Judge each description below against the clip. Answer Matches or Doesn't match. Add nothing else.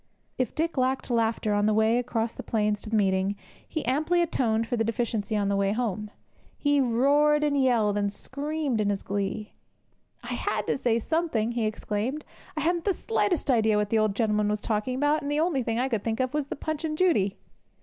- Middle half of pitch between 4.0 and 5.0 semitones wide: Doesn't match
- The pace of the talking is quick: Matches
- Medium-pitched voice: Doesn't match